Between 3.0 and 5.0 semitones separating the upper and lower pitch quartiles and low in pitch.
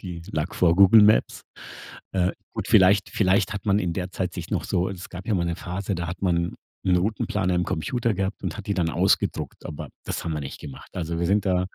No: narrow, 2.4 semitones; very low, 90 Hz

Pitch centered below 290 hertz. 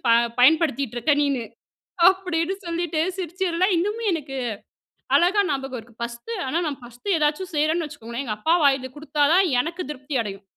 No: very high, 300 Hz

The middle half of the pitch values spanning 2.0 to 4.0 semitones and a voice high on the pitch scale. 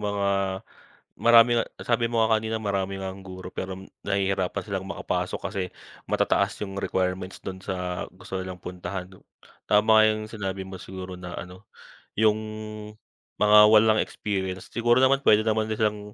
No: narrow, 2.5 semitones; low, 100 Hz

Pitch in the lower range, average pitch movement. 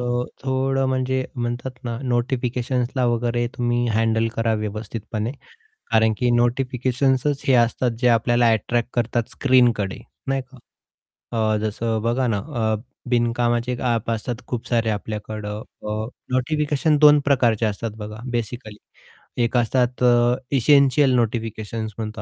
No: low, 120 Hz; narrow, 2.2 semitones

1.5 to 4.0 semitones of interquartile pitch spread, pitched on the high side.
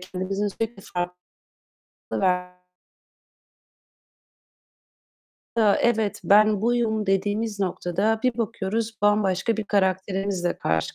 Yes: average, 2.7 semitones; high, 200 Hz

